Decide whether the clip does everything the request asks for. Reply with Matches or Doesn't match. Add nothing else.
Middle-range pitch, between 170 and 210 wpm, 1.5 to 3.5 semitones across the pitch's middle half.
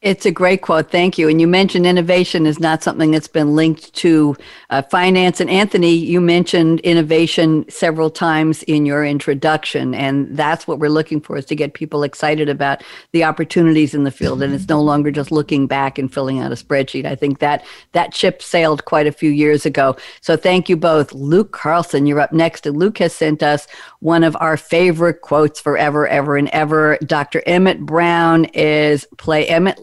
Matches